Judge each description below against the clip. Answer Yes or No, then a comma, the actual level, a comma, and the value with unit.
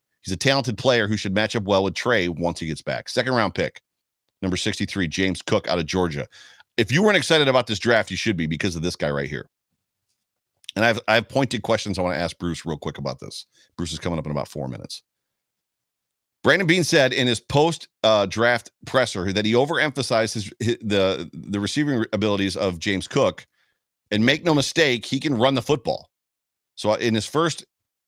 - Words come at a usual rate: No, fast, 210 wpm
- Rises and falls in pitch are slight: No, average, 5.0 semitones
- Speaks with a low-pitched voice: Yes, low, 110 Hz